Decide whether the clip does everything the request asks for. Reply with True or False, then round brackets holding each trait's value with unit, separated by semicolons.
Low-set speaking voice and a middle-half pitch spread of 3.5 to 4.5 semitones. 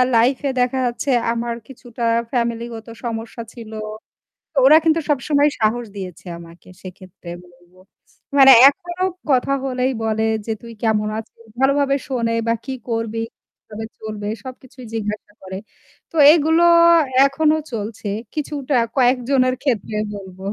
False (235 Hz; 3.8 semitones)